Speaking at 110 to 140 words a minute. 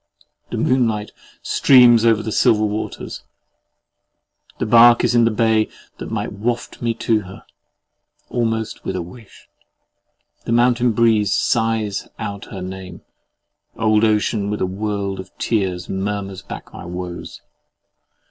Yes: slow, 135 wpm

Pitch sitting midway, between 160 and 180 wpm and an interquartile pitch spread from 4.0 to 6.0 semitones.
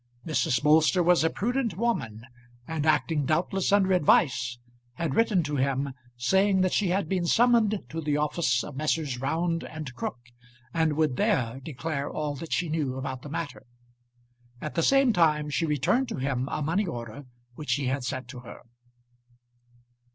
Yes: medium, 155 Hz; average, 170 wpm; average, 4.8 semitones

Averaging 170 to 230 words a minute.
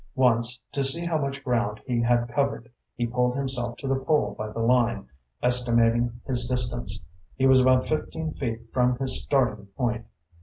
Yes: average, 175 wpm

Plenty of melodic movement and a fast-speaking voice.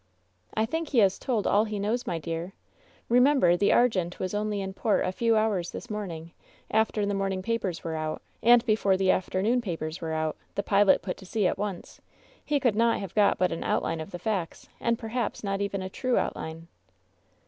No: average, 3.8 semitones; fast, 215 wpm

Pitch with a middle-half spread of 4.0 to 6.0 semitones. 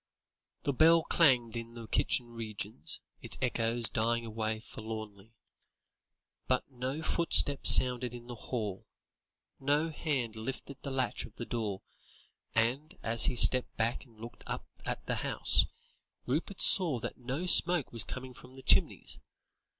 No: average, 3.0 semitones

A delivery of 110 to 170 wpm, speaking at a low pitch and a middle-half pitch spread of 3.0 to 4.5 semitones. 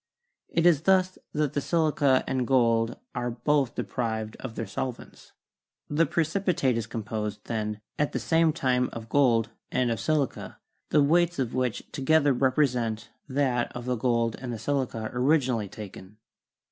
Yes: average, 160 wpm; low, 125 Hz; average, 4.2 semitones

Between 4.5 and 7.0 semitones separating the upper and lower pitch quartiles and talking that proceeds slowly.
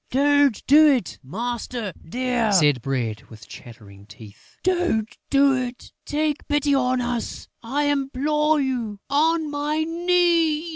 Yes: wide, 5.6 semitones; slow, 130 wpm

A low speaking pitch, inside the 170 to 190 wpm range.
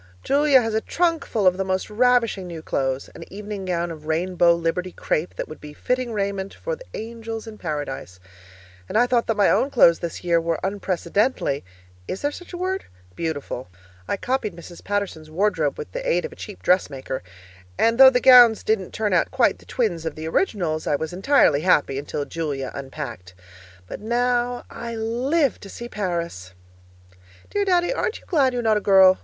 No: high, 200 Hz; average, 185 wpm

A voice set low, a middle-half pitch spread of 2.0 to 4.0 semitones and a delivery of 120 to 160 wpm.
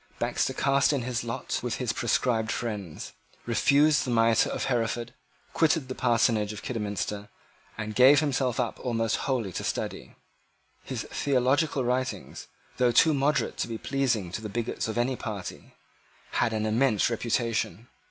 Yes: low, 120 Hz; average, 3.1 semitones; average, 150 wpm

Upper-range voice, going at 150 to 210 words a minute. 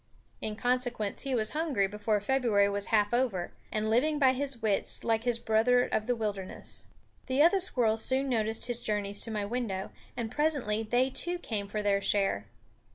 Yes: high, 225 Hz; average, 180 wpm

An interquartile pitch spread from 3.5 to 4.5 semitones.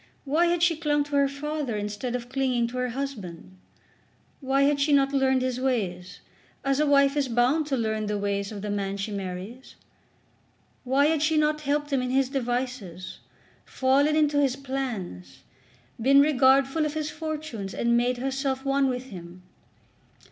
Yes: average, 4.0 semitones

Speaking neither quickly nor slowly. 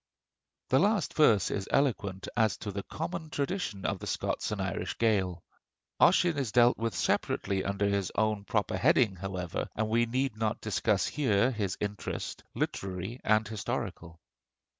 Yes: average, 155 wpm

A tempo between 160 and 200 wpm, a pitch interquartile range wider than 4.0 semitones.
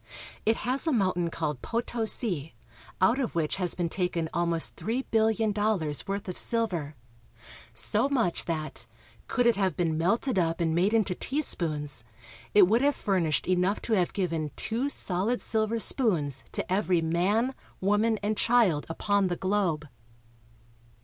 Yes: average, 165 wpm; average, 5.0 semitones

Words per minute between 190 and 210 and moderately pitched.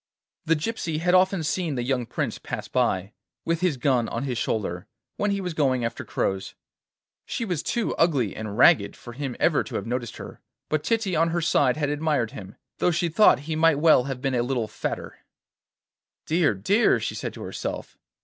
Yes: average, 195 wpm; medium, 145 Hz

